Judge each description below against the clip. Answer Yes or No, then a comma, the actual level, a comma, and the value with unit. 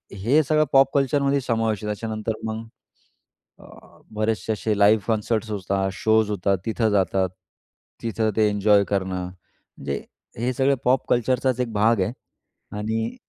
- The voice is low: Yes, low, 110 Hz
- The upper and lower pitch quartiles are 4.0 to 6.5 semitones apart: No, average, 2.7 semitones